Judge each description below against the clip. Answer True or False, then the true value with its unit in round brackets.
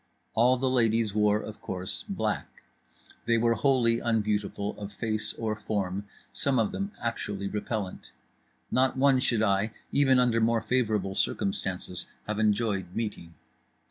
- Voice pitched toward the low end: True (110 Hz)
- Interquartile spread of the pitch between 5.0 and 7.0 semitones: False (2.5 semitones)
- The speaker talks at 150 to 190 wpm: False (140 wpm)